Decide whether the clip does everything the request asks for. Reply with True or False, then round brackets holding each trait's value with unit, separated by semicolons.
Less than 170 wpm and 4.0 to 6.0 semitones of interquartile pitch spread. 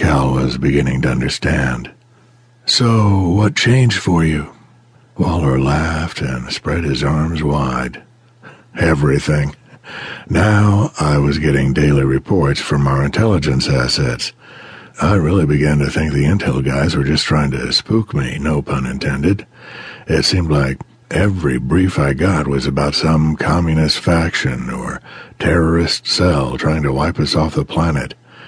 True (135 wpm; 5.0 semitones)